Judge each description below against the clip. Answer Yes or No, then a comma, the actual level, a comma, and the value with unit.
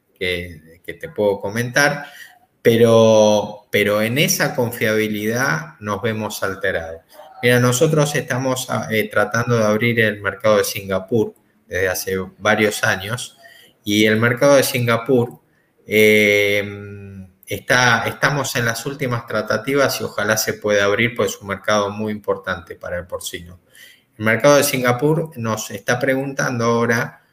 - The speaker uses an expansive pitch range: No, average, 3.4 semitones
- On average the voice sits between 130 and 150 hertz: No, low, 115 Hz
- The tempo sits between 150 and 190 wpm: No, average, 135 wpm